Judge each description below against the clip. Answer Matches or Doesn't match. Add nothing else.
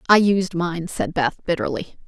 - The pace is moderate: Matches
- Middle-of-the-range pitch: Matches